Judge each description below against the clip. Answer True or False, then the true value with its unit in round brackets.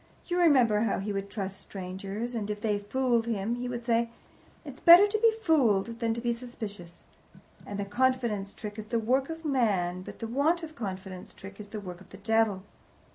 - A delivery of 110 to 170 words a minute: False (205 wpm)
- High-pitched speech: True (225 Hz)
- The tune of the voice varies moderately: True (4.0 semitones)